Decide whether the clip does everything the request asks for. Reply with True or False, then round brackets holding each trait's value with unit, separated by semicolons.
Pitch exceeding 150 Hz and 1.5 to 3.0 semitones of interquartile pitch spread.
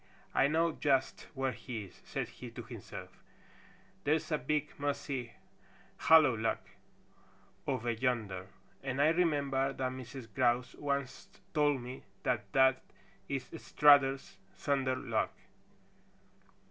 False (135 Hz; 2.5 semitones)